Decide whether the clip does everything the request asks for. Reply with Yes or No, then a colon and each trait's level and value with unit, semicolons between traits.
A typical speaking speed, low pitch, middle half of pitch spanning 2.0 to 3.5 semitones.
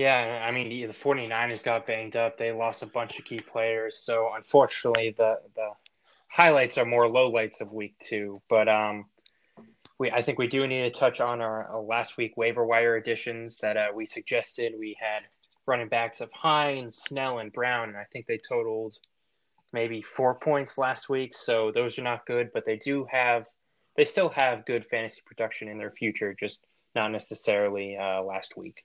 Yes: average, 190 wpm; low, 115 Hz; narrow, 2.6 semitones